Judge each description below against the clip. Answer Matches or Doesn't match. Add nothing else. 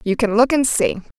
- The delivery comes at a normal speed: Doesn't match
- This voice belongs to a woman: Matches